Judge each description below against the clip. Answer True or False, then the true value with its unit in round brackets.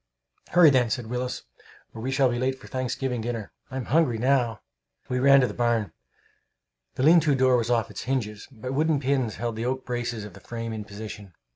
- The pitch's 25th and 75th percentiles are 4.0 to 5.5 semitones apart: False (2.7 semitones)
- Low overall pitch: True (125 Hz)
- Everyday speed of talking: False (210 wpm)